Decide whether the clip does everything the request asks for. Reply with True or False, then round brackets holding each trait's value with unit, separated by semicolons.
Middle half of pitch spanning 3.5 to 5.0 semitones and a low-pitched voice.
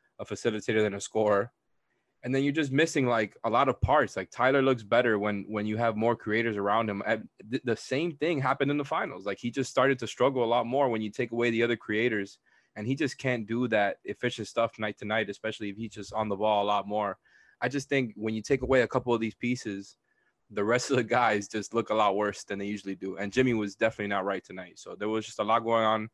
False (3.1 semitones; 110 Hz)